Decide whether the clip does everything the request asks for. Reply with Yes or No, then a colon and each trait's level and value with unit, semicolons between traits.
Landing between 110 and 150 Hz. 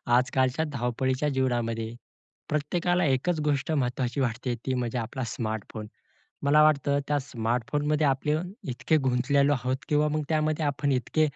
Yes: low, 135 Hz